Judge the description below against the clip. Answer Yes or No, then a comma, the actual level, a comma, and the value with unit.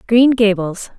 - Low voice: No, high, 215 Hz